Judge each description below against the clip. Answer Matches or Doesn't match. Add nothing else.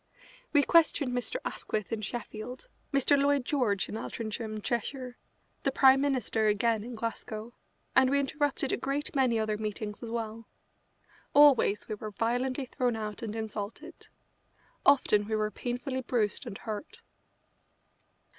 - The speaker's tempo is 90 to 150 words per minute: Matches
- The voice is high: Matches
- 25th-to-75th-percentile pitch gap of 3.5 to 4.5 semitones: Matches